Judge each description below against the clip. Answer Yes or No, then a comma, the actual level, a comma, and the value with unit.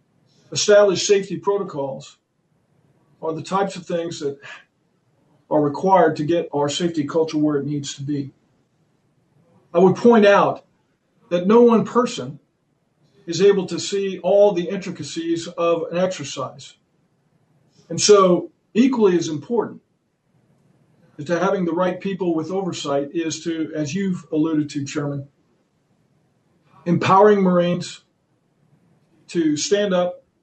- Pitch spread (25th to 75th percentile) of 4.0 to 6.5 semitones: No, average, 3.3 semitones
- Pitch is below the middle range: No, medium, 165 Hz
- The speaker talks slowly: Yes, slow, 125 wpm